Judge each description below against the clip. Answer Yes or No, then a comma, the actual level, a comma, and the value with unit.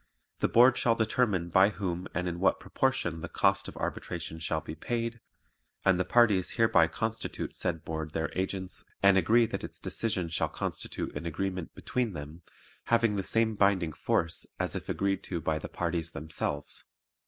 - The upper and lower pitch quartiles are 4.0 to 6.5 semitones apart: Yes, average, 5.2 semitones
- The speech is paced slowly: No, average, 175 wpm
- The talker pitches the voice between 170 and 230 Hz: No, very low, 95 Hz